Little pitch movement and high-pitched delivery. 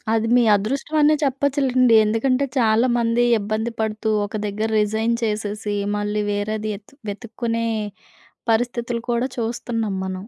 Yes: narrow, 2.3 semitones; high, 225 Hz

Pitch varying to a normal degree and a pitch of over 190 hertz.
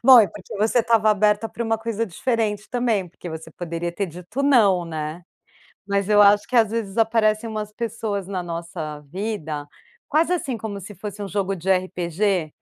Yes: average, 3.9 semitones; high, 205 Hz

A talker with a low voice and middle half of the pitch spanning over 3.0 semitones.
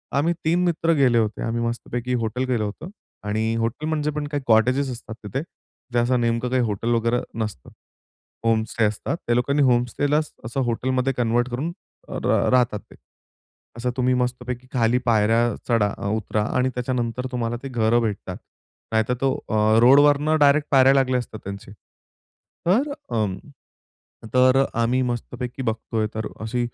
No: low, 120 Hz; narrow, 2.5 semitones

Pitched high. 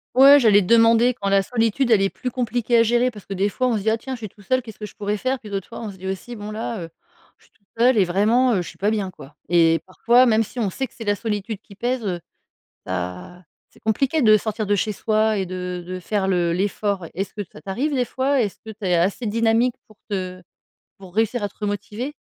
Yes: high, 215 Hz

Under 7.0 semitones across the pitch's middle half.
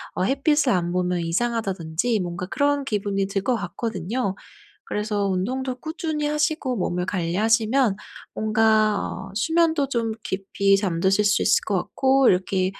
Yes: wide, 5.6 semitones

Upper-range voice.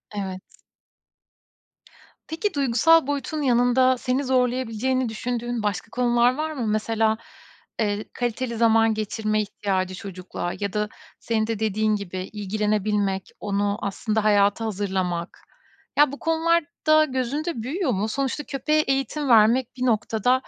Yes: high, 225 Hz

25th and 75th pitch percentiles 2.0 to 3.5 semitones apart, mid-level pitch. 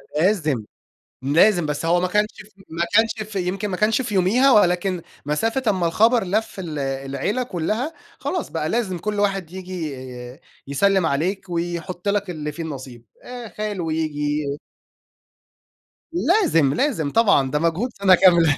No: average, 5.1 semitones; medium, 180 Hz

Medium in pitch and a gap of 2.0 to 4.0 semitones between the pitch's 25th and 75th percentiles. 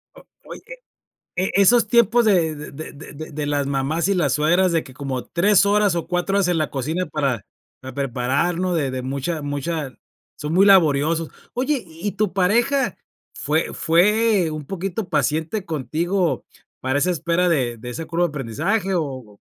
No: medium, 165 Hz; average, 4.9 semitones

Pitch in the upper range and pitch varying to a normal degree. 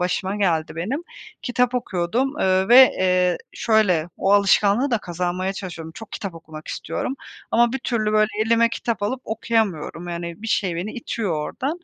Yes: high, 200 Hz; average, 4.8 semitones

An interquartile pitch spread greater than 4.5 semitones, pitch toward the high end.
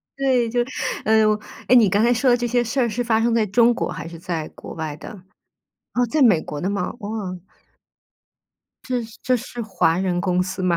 Yes: average, 4.9 semitones; high, 220 Hz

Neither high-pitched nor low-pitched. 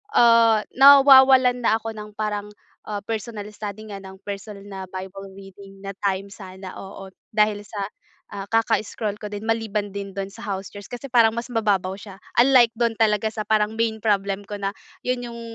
No: high, 210 Hz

